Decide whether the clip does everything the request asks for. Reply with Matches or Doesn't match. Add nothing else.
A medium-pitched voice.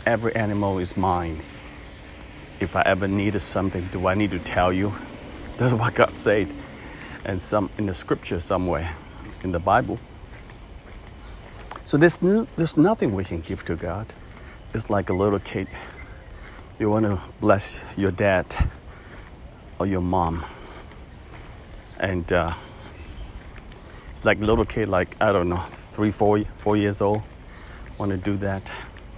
Doesn't match